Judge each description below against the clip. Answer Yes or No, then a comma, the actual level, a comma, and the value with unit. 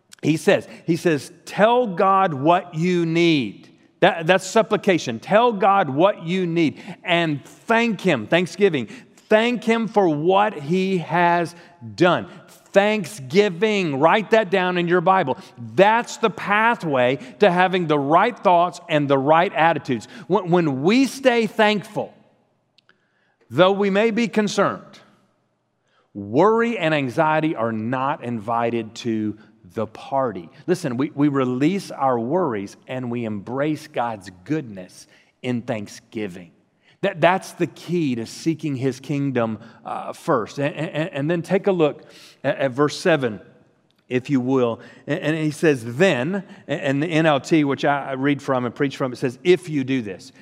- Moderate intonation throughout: No, wide, 6.0 semitones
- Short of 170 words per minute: Yes, average, 150 wpm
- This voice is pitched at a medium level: Yes, medium, 160 Hz